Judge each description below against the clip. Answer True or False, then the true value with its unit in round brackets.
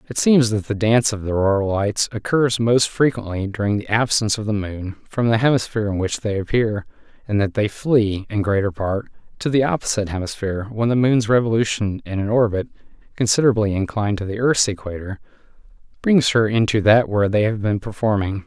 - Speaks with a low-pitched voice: True (110 Hz)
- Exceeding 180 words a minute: True (190 wpm)